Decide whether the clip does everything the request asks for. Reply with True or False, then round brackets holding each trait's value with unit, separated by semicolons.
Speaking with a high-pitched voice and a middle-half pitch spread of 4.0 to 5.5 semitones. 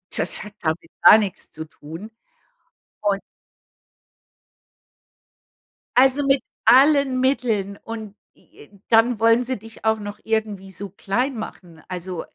True (215 Hz; 4.3 semitones)